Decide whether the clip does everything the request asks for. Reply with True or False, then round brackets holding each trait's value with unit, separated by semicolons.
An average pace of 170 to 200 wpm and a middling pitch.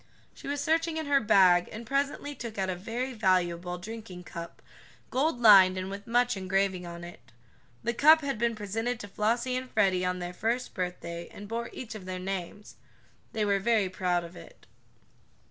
False (185 wpm; 205 Hz)